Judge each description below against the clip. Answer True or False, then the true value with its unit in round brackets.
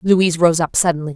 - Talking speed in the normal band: False (210 wpm)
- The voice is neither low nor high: True (170 Hz)